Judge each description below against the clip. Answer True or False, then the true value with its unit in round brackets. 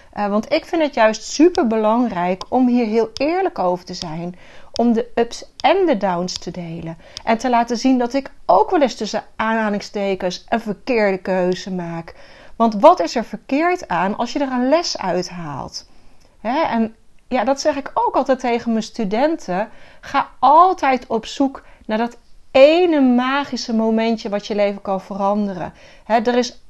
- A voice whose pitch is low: False (230 Hz)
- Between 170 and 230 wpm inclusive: True (175 wpm)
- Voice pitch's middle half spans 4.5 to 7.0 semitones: True (5.0 semitones)